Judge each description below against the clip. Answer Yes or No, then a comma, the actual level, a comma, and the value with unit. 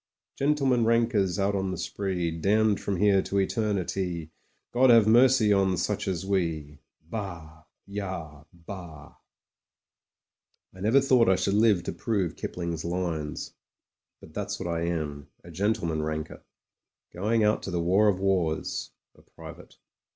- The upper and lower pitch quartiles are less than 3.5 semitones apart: No, average, 4.0 semitones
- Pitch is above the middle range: No, very low, 95 Hz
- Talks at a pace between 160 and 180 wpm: No, average, 150 wpm